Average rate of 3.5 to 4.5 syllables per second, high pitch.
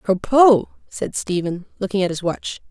No: 4.8 syllables/s; high, 200 Hz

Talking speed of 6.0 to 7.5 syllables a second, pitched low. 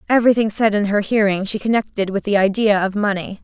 No: 6.2 syllables/s; high, 210 Hz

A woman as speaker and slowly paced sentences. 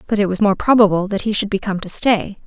No: female; fast, 290 wpm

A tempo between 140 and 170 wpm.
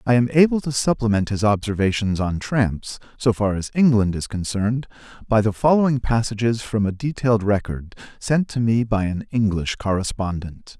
Yes: average, 165 wpm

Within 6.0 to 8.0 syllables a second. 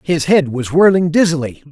No: 5.1 syllables/s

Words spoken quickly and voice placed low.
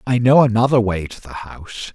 Yes: fast, 215 wpm; low, 115 Hz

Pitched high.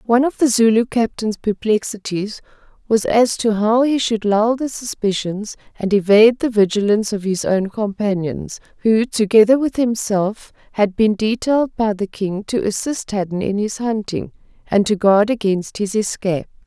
Yes: high, 215 Hz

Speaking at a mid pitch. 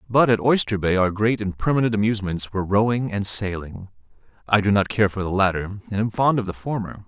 No: low, 105 Hz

